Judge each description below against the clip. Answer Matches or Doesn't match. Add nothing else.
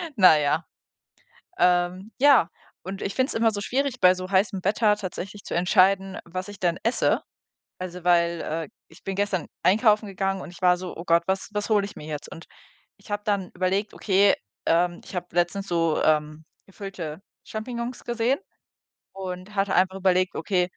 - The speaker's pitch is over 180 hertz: Matches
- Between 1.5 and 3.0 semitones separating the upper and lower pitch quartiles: Matches